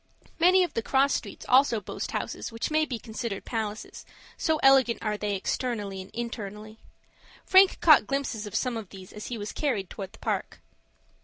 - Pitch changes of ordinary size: Yes, average, 4.6 semitones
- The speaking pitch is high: Yes, high, 230 Hz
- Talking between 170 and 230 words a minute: Yes, average, 180 wpm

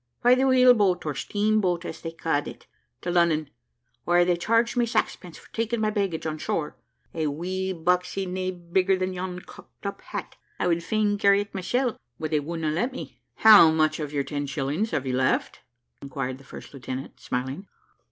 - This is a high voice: No, medium, 180 Hz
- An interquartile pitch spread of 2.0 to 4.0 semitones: No, average, 4.7 semitones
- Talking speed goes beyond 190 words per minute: Yes, average, 200 wpm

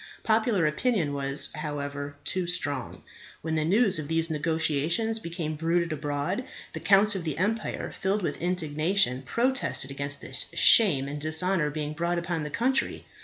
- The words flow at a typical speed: Yes, average, 155 wpm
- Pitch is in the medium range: Yes, medium, 165 Hz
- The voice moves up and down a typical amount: Yes, average, 4.6 semitones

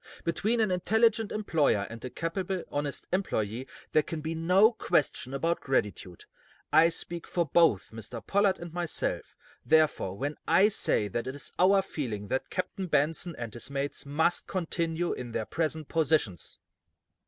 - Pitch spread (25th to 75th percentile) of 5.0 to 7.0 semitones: Yes, wide, 5.4 semitones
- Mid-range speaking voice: Yes, medium, 160 Hz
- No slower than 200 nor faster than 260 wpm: No, average, 155 wpm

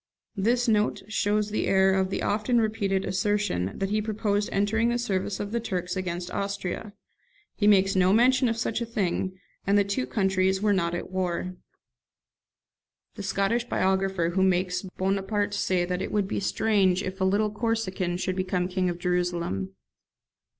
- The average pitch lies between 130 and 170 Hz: No, high, 195 Hz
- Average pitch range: No, narrow, 2.2 semitones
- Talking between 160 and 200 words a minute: Yes, average, 165 wpm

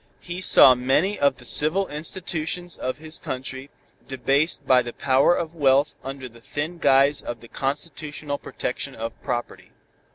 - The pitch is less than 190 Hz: Yes, medium, 140 Hz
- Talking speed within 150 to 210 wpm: Yes, average, 155 wpm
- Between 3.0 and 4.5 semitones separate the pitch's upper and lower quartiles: Yes, average, 3.3 semitones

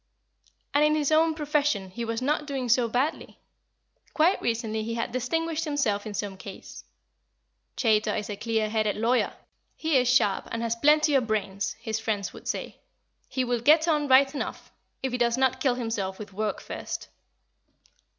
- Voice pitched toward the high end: Yes, high, 240 Hz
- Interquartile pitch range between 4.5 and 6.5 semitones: Yes, average, 5.0 semitones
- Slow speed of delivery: No, average, 175 wpm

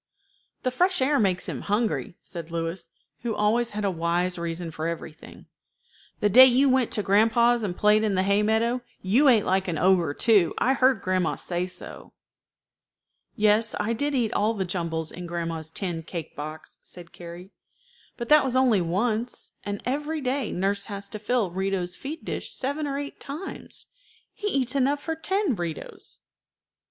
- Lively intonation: Yes, wide, 6.2 semitones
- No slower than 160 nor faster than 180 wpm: Yes, average, 175 wpm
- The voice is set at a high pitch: Yes, high, 210 Hz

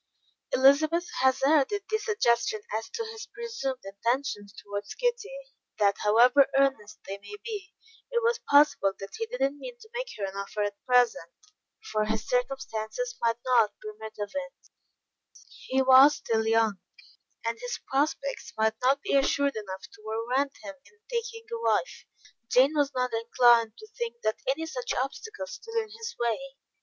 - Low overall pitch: No, very high, 265 Hz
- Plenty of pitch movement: Yes, wide, 7.8 semitones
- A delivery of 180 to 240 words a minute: No, average, 165 wpm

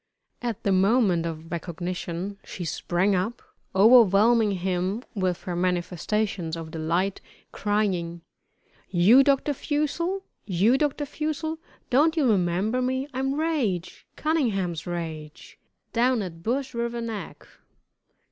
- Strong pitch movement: Yes, wide, 6.4 semitones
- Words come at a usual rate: No, slow, 115 wpm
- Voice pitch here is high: Yes, high, 200 Hz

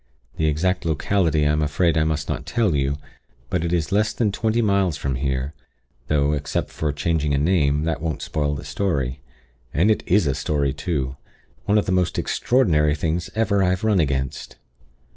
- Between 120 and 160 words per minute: No, average, 190 wpm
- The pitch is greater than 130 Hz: No, very low, 80 Hz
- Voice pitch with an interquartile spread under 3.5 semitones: No, average, 4.3 semitones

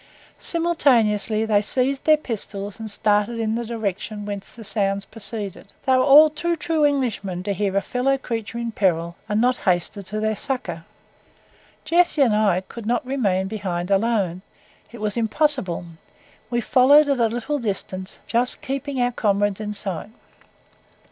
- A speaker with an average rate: Yes, average, 160 wpm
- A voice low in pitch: No, high, 220 Hz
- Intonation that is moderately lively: Yes, average, 4.3 semitones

